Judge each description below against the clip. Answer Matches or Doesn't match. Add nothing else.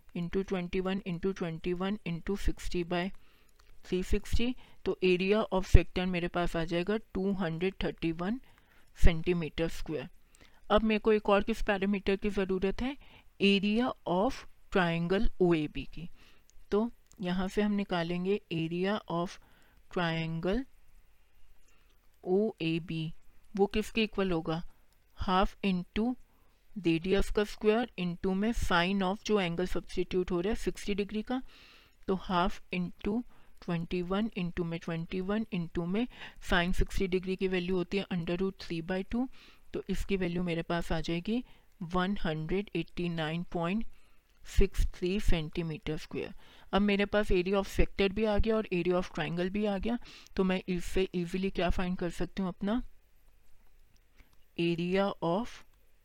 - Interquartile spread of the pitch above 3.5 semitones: Doesn't match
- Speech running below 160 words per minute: Matches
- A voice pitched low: Doesn't match